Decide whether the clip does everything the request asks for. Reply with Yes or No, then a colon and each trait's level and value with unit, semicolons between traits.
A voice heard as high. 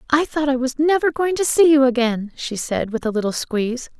Yes: very high, 270 Hz